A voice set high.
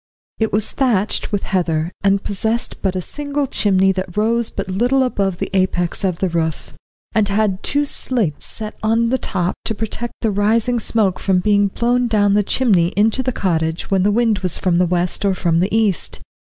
Yes: high, 205 Hz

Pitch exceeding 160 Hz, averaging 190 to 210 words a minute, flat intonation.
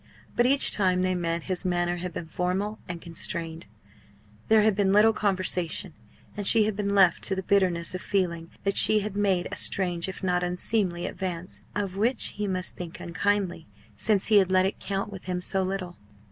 Yes: medium, 185 Hz; average, 195 wpm; narrow, 2.3 semitones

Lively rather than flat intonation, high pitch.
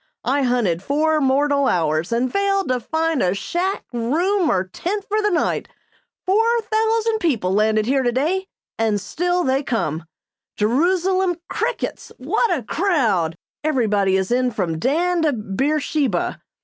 Yes: wide, 8.8 semitones; very high, 275 Hz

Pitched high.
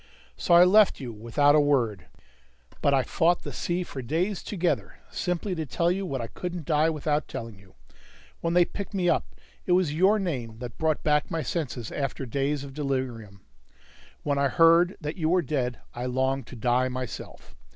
No: medium, 150 Hz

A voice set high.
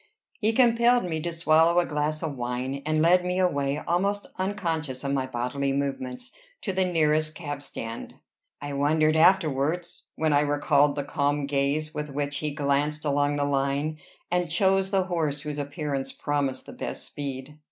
No: medium, 150 Hz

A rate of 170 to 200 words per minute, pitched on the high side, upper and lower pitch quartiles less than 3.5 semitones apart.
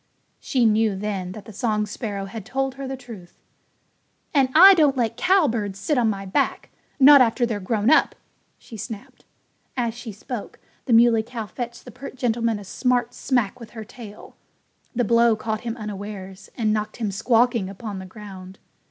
Yes: average, 180 wpm; high, 225 Hz; average, 3.0 semitones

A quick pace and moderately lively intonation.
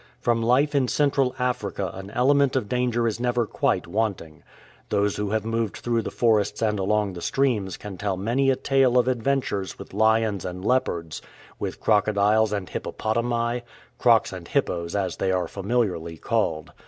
No: average, 175 wpm; average, 3.8 semitones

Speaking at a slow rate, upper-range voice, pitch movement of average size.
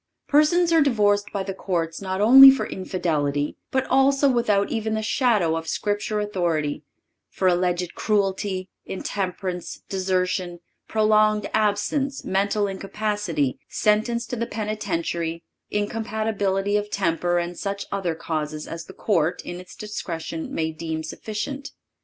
Yes: slow, 130 wpm; high, 200 Hz; average, 3.6 semitones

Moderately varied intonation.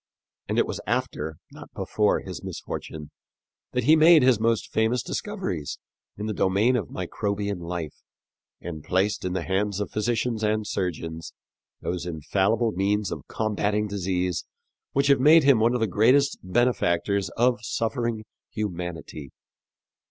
Yes: average, 4.6 semitones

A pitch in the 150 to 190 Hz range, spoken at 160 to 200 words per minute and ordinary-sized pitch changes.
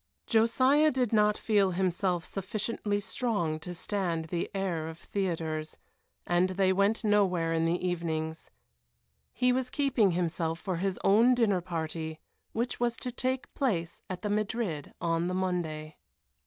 No: medium, 185 Hz; average, 145 wpm; average, 4.6 semitones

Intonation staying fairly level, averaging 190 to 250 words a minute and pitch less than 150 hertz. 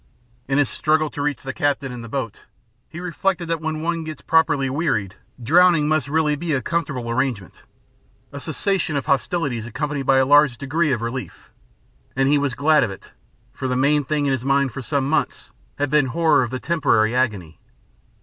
No: average, 3.2 semitones; average, 195 wpm; medium, 140 Hz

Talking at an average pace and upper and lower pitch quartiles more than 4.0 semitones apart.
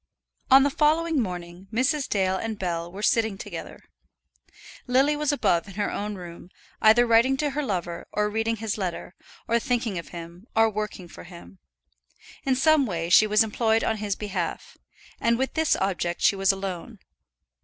Yes: average, 175 wpm; average, 5.0 semitones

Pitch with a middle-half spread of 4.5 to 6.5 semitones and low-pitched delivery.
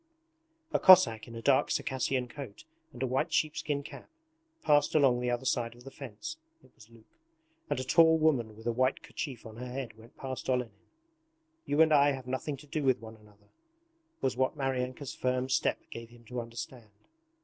No: average, 2.8 semitones; low, 125 Hz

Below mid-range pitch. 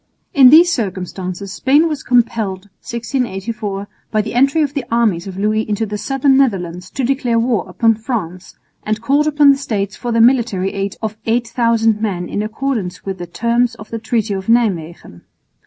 No: high, 225 Hz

